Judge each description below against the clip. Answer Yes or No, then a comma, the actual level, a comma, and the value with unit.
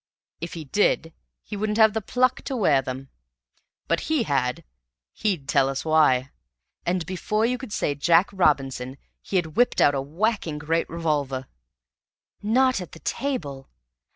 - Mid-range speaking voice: Yes, medium, 165 Hz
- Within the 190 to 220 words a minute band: No, average, 155 wpm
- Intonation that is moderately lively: No, wide, 7.3 semitones